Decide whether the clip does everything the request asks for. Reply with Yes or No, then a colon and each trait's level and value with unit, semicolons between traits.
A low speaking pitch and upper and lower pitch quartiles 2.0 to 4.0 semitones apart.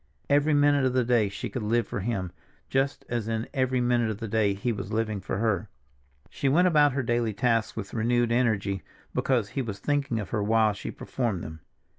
Yes: low, 115 Hz; average, 3.4 semitones